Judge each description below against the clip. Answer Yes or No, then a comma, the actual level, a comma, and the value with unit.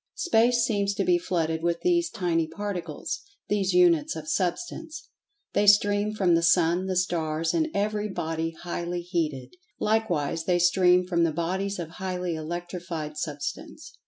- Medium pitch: Yes, medium, 180 Hz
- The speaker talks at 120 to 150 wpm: Yes, average, 145 wpm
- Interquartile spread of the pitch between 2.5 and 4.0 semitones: Yes, average, 3.7 semitones